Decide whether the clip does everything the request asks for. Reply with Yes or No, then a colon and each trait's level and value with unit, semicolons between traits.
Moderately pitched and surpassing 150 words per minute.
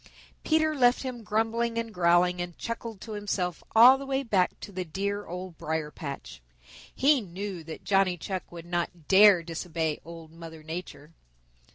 Yes: medium, 180 Hz; average, 165 wpm